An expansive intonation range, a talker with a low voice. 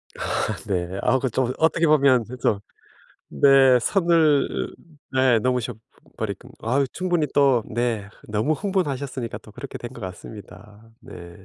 No: average, 4.8 semitones; low, 125 Hz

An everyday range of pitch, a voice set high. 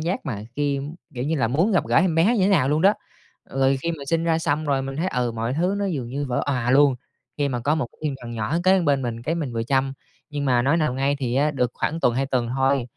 No: average, 4.2 semitones; medium, 140 Hz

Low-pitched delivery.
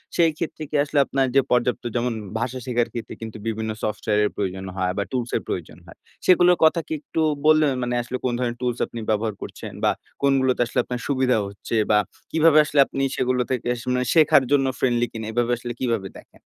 Yes: low, 125 Hz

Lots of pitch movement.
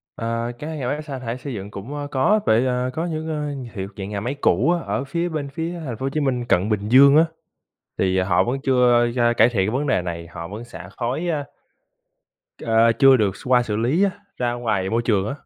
No: average, 4.7 semitones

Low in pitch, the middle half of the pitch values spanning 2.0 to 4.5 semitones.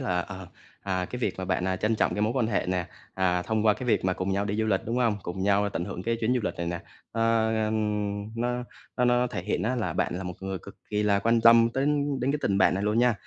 Yes: low, 105 Hz; average, 3.4 semitones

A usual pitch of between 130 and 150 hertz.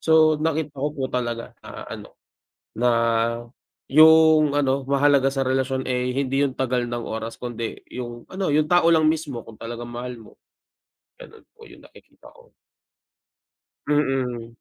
Yes: low, 135 Hz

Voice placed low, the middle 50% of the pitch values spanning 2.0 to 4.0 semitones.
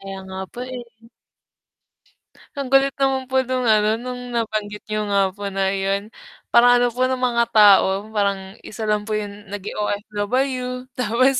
No: high, 220 Hz; average, 3.6 semitones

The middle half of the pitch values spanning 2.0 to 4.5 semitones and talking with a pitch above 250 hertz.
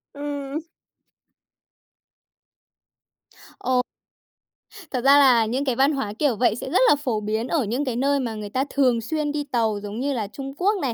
Yes: average, 3.7 semitones; very high, 260 Hz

